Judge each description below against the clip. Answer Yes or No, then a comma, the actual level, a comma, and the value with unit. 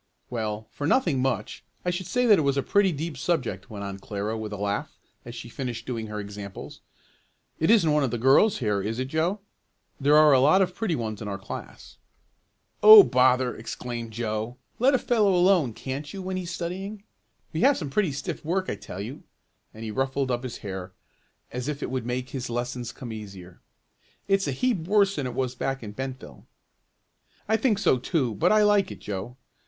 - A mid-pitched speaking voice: No, low, 130 Hz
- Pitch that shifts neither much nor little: No, wide, 7.9 semitones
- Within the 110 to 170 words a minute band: No, fast, 205 wpm